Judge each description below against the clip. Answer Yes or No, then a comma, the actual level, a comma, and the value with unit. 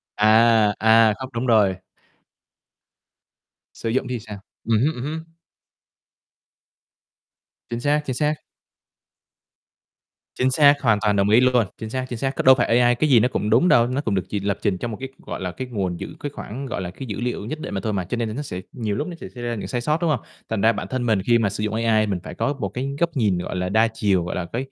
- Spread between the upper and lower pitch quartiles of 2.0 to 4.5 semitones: Yes, average, 3.8 semitones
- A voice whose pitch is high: No, low, 115 Hz